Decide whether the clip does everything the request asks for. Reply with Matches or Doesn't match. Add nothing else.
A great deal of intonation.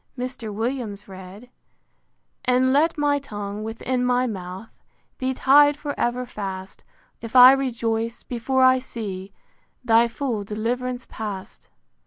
Doesn't match